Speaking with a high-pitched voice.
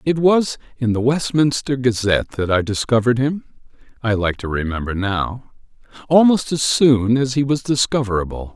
No: low, 125 Hz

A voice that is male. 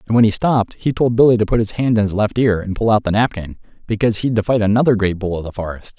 Yes: male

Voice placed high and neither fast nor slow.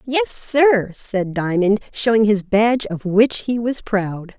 Yes: high, 215 Hz; average, 165 wpm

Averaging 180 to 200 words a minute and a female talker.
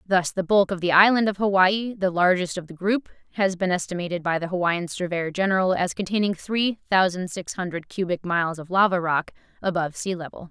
Yes: average, 195 wpm; female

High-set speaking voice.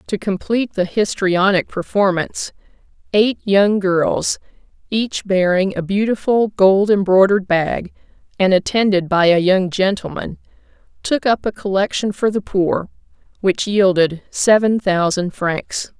Yes: high, 195 Hz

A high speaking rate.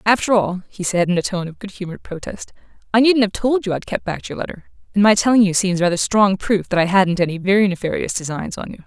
Yes: fast, 255 wpm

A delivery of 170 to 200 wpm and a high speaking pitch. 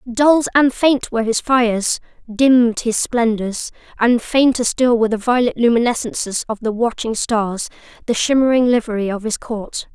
No: average, 155 wpm; high, 235 Hz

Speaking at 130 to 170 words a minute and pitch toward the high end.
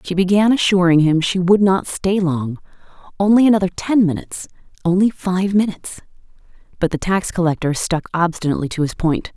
No: average, 160 wpm; medium, 180 Hz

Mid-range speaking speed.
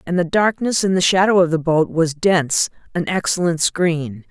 Yes: average, 195 wpm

